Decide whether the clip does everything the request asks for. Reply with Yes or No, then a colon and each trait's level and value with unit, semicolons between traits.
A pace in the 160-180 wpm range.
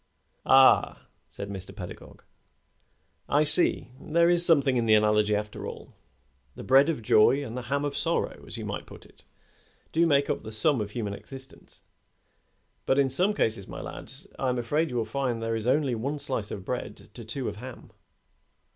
No: average, 190 wpm